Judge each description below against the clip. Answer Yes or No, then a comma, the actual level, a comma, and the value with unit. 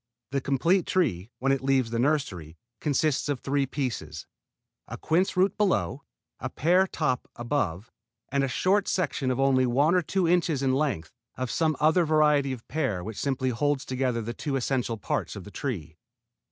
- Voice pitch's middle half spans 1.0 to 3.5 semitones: No, average, 4.4 semitones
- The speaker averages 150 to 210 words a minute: Yes, average, 180 wpm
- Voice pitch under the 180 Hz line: Yes, low, 135 Hz